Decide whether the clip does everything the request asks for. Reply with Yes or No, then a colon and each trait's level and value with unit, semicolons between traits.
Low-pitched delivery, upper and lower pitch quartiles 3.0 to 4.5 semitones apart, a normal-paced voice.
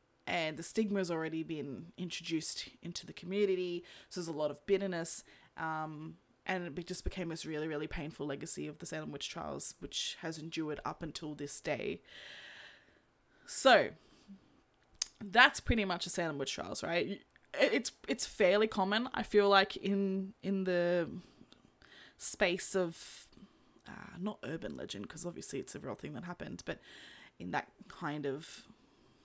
No: medium, 175 Hz; average, 3.6 semitones; average, 155 wpm